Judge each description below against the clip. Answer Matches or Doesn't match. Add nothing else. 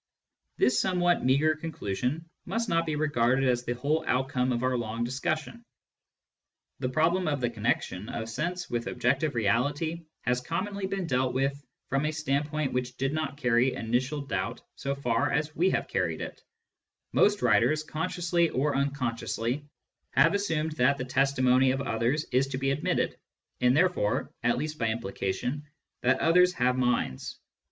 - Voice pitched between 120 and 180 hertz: Matches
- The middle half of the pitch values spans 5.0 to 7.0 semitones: Doesn't match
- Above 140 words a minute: Matches